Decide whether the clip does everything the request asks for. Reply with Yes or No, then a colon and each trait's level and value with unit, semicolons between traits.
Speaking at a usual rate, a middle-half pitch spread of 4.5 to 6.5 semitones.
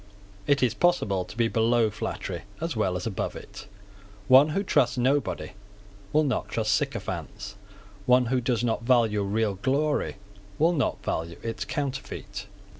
Yes: average, 150 wpm; average, 4.8 semitones